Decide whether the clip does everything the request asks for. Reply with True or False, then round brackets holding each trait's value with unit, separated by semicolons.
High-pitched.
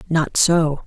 False (160 Hz)